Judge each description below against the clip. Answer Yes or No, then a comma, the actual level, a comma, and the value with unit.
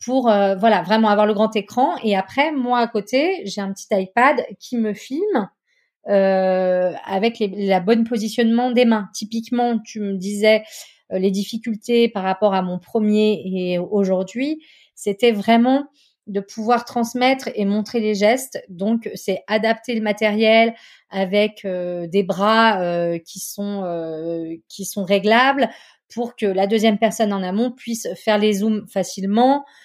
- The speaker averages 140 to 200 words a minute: Yes, average, 160 wpm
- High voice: Yes, high, 215 Hz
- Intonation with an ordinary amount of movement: Yes, average, 3.2 semitones